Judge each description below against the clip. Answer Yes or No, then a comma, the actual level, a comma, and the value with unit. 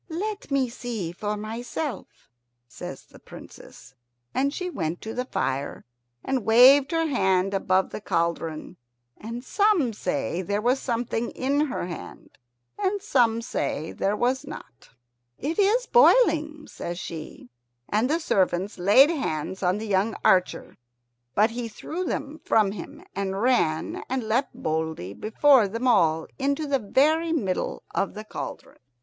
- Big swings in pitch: Yes, wide, 6.8 semitones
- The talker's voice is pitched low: No, high, 230 Hz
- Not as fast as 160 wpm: Yes, average, 145 wpm